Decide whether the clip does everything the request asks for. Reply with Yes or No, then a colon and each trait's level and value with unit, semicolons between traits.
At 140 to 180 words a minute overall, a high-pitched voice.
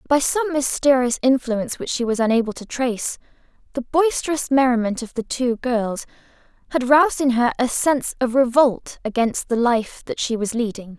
Yes: average, 175 wpm; very high, 250 Hz